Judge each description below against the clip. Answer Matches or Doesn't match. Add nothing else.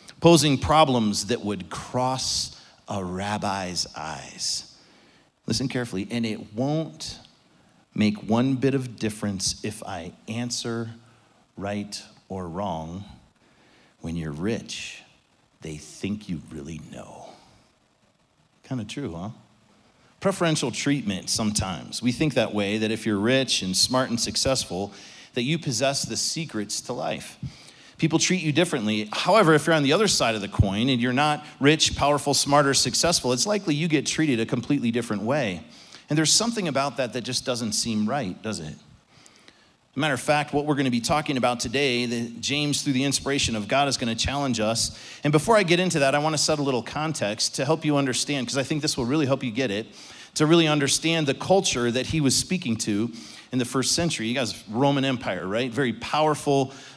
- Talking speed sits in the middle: Matches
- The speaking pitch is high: Doesn't match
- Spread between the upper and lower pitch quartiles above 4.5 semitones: Matches